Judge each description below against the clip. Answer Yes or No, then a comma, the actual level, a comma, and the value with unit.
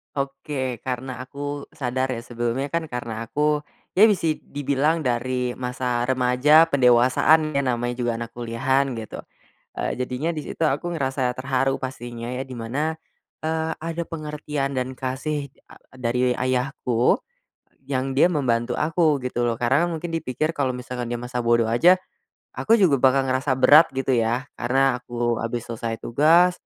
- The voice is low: Yes, low, 130 Hz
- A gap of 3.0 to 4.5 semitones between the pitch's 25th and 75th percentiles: Yes, average, 3.4 semitones